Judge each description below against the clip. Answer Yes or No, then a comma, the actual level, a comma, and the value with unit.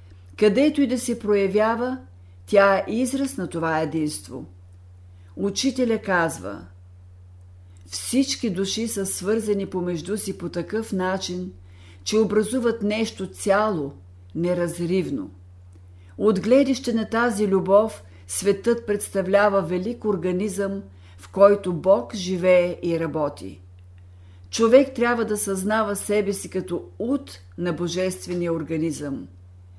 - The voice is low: No, medium, 185 Hz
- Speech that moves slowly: Yes, slow, 105 wpm